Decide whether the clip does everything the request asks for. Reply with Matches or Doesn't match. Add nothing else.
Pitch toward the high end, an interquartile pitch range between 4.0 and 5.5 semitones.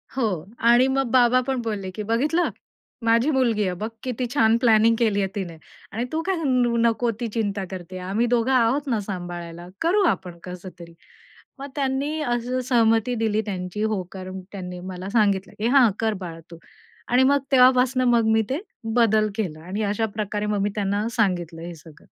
Matches